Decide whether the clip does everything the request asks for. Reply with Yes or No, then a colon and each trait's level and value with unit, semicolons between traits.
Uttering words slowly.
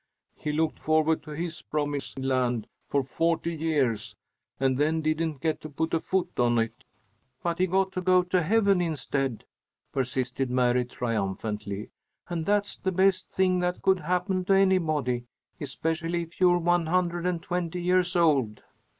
No: average, 155 wpm